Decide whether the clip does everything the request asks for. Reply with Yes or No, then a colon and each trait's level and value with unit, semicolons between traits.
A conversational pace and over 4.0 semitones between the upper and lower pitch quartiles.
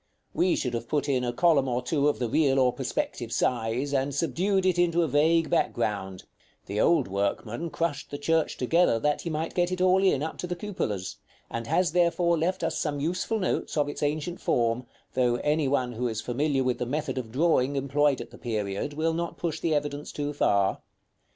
No: fast, 210 wpm; average, 5.2 semitones